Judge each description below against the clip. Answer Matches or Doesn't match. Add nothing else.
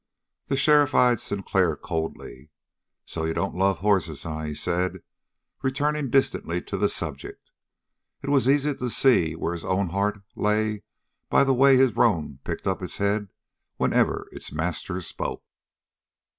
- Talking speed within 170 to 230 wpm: Doesn't match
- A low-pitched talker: Matches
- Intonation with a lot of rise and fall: Matches